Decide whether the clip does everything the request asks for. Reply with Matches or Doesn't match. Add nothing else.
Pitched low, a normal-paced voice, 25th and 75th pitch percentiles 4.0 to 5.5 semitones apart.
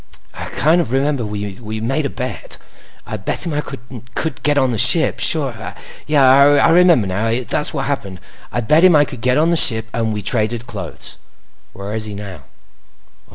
Matches